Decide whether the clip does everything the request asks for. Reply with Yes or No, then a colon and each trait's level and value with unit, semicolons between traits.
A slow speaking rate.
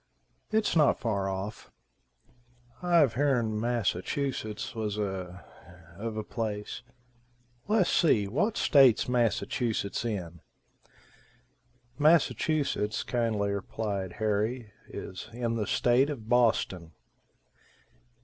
Yes: slow, 90 wpm